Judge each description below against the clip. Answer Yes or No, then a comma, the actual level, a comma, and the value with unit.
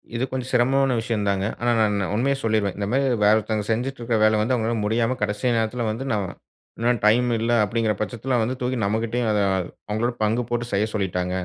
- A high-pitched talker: No, low, 115 Hz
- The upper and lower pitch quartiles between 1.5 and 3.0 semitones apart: Yes, narrow, 2.5 semitones